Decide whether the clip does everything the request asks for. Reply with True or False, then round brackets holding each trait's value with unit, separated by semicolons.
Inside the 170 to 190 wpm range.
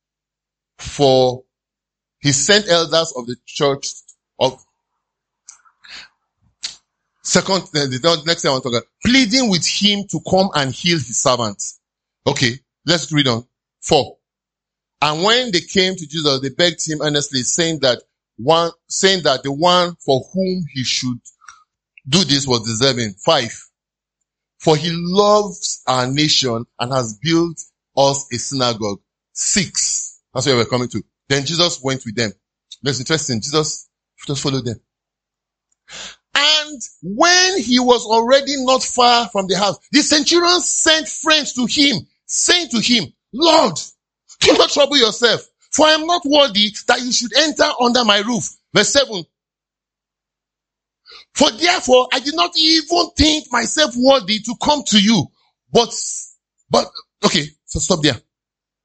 False (145 wpm)